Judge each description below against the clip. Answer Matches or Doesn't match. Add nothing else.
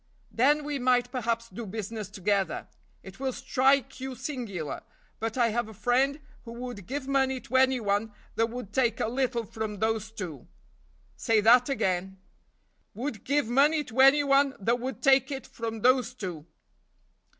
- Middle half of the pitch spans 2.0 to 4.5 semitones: Matches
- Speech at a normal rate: Matches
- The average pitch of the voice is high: Matches